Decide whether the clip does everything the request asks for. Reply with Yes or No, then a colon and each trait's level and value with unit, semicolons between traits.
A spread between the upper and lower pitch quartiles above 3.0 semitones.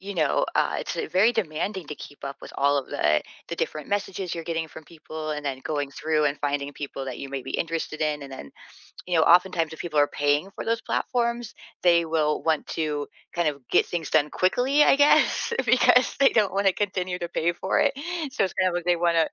Yes: average, 4.2 semitones